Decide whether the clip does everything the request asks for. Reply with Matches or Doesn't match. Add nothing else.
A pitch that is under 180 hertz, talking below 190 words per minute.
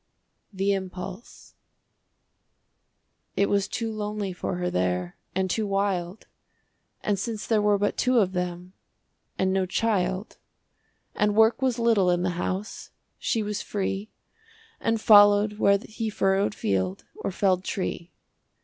Doesn't match